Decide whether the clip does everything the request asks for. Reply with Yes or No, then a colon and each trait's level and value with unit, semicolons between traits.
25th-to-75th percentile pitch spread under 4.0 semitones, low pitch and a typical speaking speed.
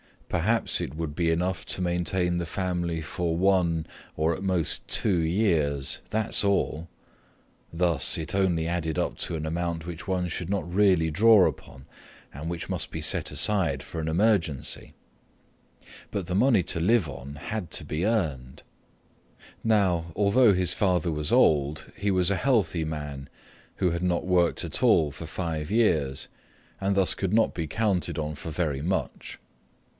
Yes: average, 3.2 semitones; very low, 85 Hz; average, 165 wpm